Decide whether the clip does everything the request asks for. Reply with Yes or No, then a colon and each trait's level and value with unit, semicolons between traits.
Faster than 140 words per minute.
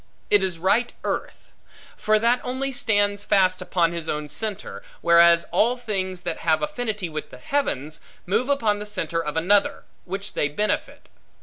Yes: average, 165 wpm